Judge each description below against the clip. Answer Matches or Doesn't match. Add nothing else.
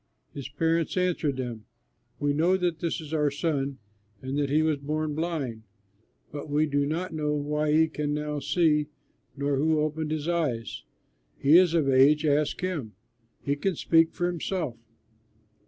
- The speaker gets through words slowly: Doesn't match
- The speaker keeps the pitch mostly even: Matches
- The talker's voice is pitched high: Doesn't match